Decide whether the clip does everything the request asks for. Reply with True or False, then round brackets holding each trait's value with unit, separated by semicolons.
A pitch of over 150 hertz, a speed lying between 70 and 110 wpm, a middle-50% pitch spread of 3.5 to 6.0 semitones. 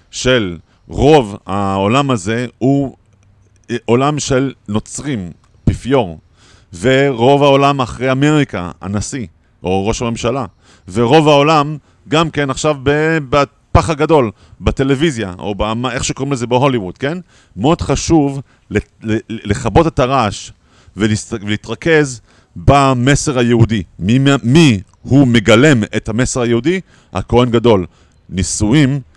False (120 Hz; 105 wpm; 5.2 semitones)